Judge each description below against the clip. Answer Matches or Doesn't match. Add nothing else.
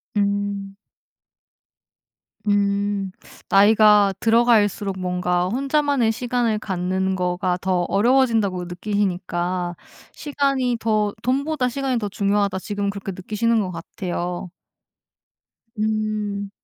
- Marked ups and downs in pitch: Doesn't match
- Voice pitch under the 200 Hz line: Doesn't match